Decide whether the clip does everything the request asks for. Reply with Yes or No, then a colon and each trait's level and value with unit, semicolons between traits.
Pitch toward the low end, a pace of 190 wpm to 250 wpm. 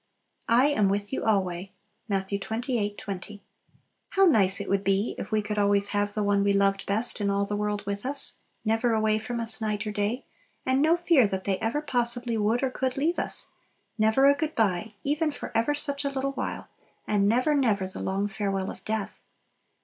No: high, 215 Hz; fast, 205 wpm